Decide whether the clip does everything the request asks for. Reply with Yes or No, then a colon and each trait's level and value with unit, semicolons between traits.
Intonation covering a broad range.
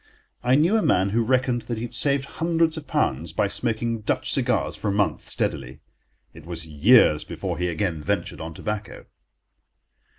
Yes: wide, 6.6 semitones